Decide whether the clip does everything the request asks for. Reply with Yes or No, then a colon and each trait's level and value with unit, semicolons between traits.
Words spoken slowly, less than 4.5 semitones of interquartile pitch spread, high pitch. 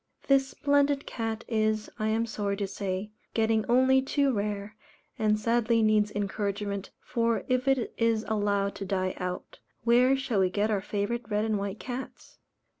No: average, 165 wpm; average, 2.8 semitones; high, 215 Hz